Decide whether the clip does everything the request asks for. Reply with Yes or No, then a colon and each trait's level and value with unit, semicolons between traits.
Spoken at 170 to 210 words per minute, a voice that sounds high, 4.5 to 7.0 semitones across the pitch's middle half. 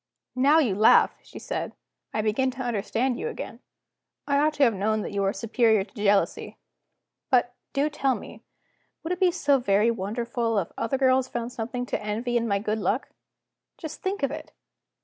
No: average, 190 wpm; high, 240 Hz; average, 4.1 semitones